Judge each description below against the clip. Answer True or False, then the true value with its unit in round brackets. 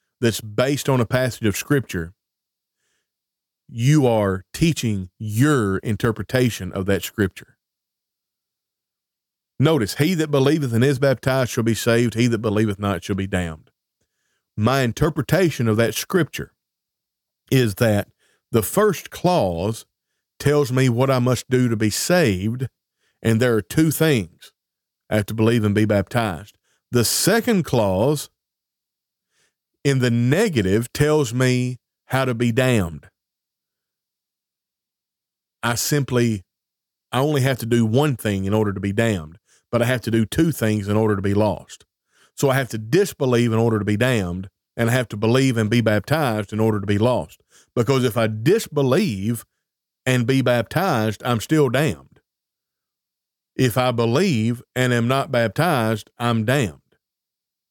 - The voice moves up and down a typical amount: True (3.9 semitones)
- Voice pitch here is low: True (120 Hz)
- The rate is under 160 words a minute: True (150 wpm)